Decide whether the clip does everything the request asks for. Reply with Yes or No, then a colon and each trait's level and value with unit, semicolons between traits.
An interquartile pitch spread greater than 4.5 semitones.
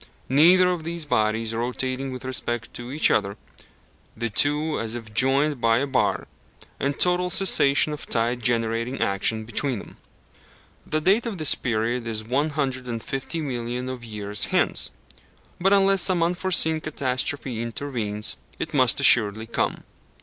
Yes: average, 5.0 semitones